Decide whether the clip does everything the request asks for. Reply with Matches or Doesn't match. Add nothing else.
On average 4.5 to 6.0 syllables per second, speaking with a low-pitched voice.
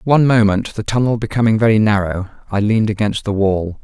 Doesn't match